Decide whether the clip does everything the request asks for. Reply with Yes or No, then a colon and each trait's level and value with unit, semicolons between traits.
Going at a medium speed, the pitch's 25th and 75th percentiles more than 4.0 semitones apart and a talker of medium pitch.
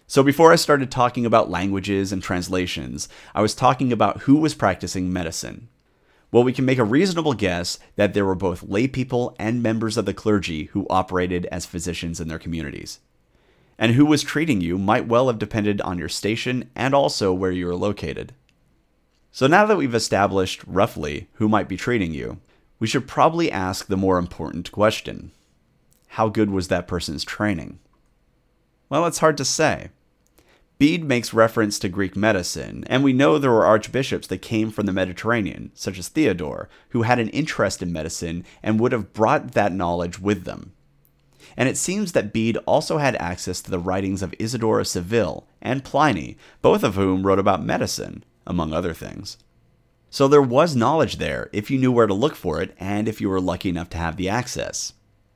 No: average, 185 wpm; average, 5.0 semitones; low, 105 Hz